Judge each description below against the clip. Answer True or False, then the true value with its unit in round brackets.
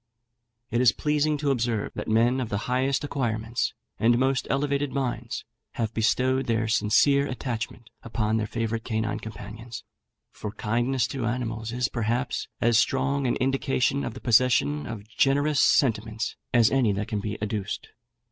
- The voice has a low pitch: True (120 Hz)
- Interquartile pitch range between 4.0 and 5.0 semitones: False (3.3 semitones)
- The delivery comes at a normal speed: True (155 wpm)